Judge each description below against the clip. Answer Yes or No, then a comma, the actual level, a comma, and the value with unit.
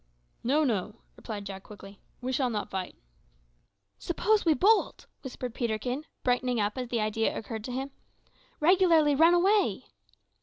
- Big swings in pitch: Yes, wide, 6.3 semitones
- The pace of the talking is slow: No, average, 145 wpm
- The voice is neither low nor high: No, very high, 250 Hz